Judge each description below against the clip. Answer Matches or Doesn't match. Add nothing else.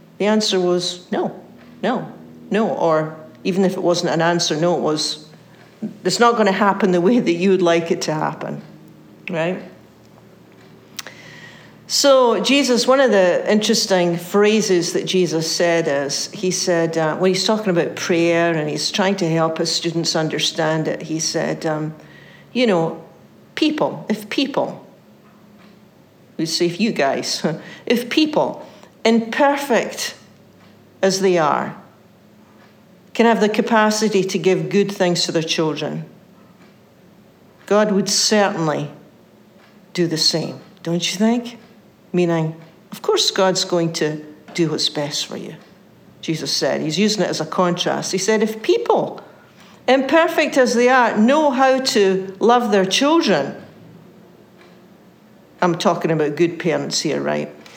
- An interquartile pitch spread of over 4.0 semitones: Matches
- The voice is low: Doesn't match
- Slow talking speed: Doesn't match